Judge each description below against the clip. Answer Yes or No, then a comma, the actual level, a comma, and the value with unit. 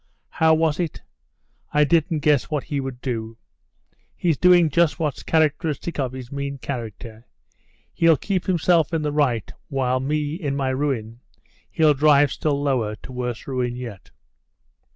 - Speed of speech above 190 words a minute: No, average, 150 wpm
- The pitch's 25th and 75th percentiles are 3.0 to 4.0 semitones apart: Yes, average, 3.7 semitones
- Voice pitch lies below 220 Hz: Yes, medium, 140 Hz